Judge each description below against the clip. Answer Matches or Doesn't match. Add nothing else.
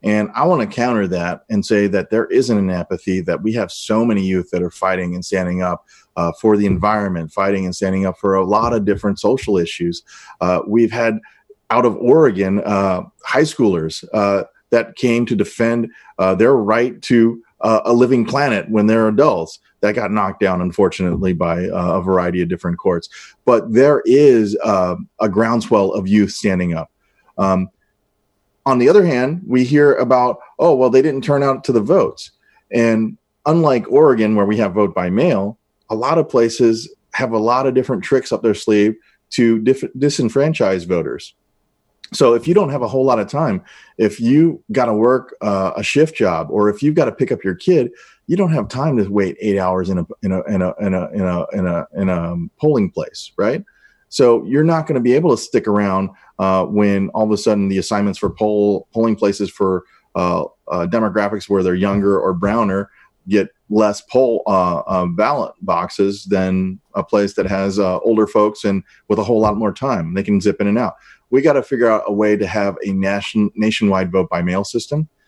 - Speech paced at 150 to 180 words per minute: Doesn't match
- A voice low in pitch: Matches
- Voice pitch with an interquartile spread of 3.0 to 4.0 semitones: Matches